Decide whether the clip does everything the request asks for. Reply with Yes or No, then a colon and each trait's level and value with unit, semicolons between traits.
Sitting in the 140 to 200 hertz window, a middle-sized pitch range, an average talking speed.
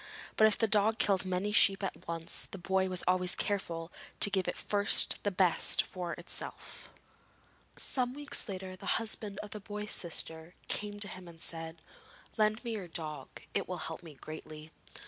Yes: high, 190 Hz; average, 3.5 semitones; average, 180 wpm